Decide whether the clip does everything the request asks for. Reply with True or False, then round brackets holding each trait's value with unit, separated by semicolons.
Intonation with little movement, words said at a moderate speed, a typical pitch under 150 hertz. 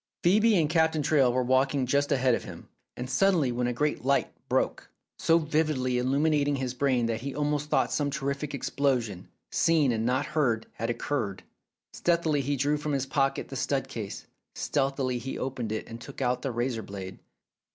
False (3.1 semitones; 180 wpm; 135 Hz)